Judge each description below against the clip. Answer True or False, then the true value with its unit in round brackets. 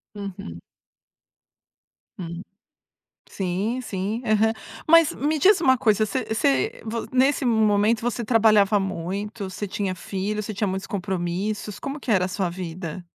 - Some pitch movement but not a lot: True (3.3 semitones)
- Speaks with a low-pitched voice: False (205 Hz)